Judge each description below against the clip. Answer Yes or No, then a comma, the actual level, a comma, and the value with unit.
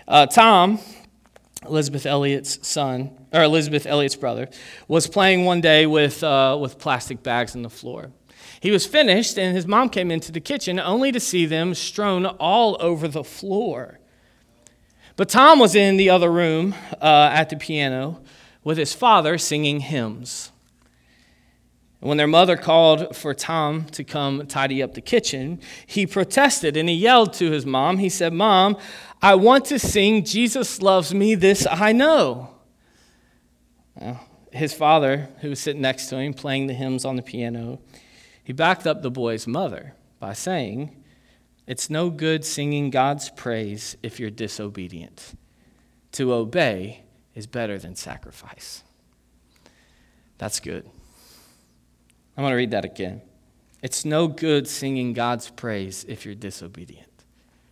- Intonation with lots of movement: Yes, wide, 6.5 semitones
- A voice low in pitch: No, medium, 145 Hz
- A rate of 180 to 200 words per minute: No, average, 150 wpm